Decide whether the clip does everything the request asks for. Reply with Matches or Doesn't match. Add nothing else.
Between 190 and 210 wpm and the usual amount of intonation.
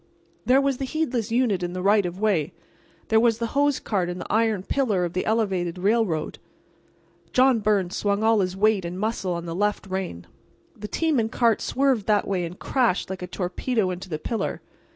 Matches